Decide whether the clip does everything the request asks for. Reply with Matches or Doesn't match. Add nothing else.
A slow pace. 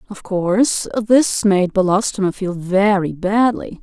Matches